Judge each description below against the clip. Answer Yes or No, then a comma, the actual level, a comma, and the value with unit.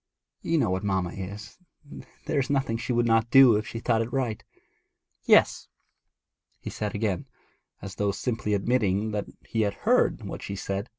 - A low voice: Yes, low, 110 Hz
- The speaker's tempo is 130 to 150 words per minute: No, average, 175 wpm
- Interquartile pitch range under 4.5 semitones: Yes, average, 3.0 semitones